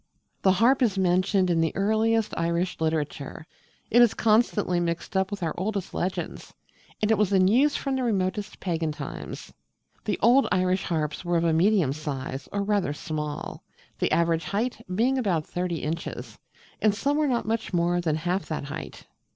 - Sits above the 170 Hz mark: Yes, medium, 185 Hz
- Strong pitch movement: No, average, 4.5 semitones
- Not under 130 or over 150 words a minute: No, average, 175 wpm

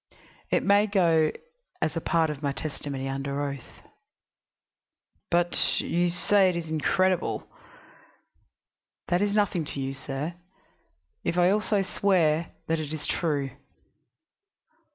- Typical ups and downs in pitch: Yes, average, 4.2 semitones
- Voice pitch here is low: No, medium, 165 Hz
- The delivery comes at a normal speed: No, slow, 125 wpm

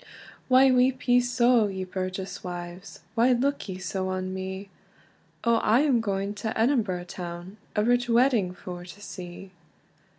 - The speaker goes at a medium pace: Yes, average, 155 wpm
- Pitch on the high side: Yes, high, 200 Hz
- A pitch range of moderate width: Yes, average, 4.6 semitones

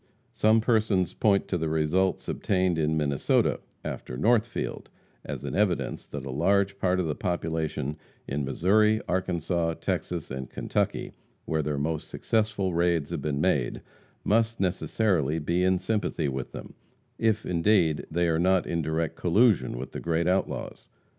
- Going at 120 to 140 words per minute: No, average, 155 wpm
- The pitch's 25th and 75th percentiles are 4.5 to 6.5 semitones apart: No, average, 4.1 semitones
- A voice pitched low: Yes, very low, 85 Hz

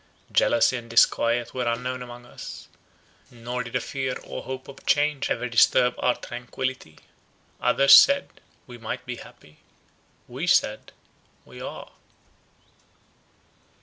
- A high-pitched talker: No, low, 125 Hz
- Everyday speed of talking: No, slow, 115 wpm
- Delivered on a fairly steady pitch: Yes, narrow, 1.7 semitones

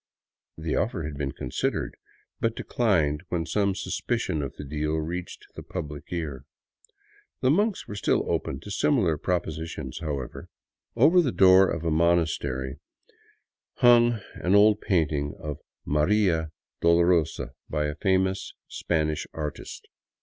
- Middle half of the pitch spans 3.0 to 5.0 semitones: Yes, average, 4.7 semitones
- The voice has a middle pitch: No, very low, 85 Hz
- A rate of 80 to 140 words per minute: Yes, slow, 135 wpm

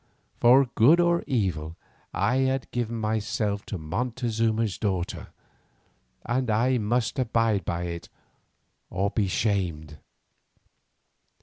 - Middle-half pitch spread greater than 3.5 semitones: Yes, average, 4.4 semitones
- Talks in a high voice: No, low, 110 Hz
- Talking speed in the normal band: No, slow, 105 wpm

